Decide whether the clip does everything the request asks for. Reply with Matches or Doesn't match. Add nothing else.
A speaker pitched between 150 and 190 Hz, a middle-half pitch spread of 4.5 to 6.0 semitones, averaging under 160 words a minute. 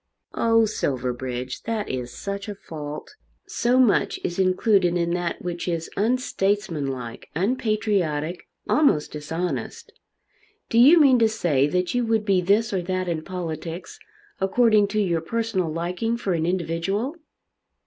Matches